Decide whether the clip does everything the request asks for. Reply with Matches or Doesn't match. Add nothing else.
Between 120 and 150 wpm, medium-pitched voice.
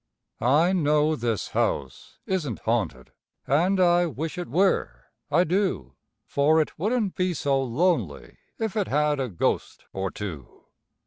Matches